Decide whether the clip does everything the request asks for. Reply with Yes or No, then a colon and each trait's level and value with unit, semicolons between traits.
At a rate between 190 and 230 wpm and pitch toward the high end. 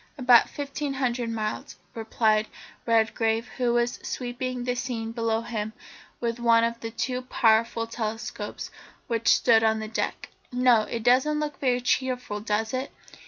No: average, 150 wpm; high, 235 Hz